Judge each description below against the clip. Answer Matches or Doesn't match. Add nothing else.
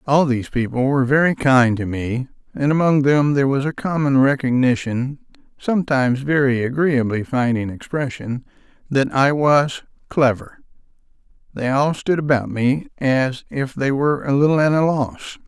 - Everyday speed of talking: Matches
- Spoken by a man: Matches